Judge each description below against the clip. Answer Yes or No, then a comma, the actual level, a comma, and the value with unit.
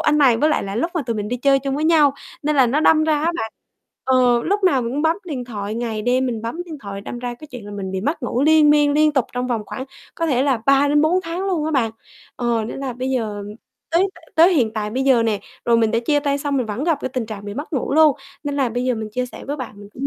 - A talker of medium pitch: No, very high, 260 Hz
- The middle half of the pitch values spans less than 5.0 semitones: Yes, average, 4.4 semitones